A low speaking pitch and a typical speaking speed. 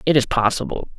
Yes: low, 130 Hz; average, 180 wpm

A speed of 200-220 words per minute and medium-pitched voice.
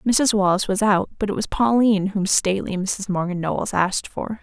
No: fast, 205 wpm; high, 200 Hz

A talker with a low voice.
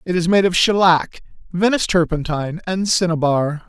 No: medium, 175 Hz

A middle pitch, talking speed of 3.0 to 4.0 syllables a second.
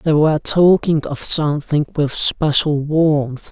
Yes: medium, 150 Hz; 3.9 syllables/s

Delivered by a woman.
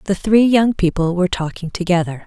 Yes: female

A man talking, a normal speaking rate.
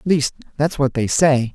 No: male; fast, 235 wpm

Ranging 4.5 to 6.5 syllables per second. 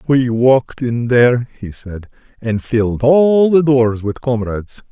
No: 4.2 syllables/s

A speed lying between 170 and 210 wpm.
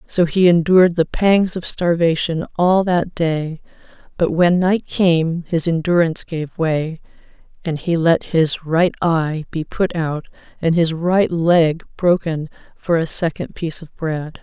No: average, 160 wpm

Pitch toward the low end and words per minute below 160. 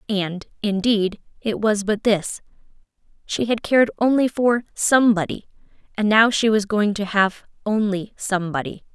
No: high, 210 Hz; average, 140 wpm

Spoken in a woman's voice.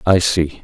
No: male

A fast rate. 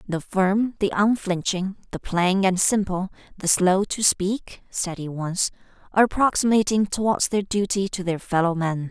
No: average, 160 wpm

